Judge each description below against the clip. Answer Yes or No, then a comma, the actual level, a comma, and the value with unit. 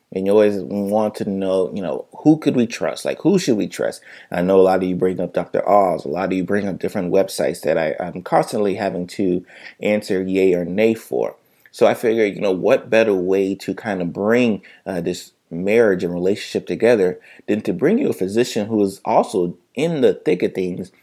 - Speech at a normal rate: No, fast, 225 wpm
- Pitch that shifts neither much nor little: No, narrow, 2.0 semitones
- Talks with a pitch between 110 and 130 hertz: No, very low, 95 Hz